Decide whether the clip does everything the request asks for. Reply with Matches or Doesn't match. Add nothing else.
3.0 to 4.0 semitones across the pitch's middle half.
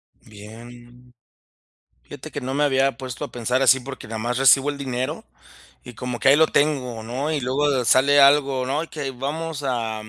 Doesn't match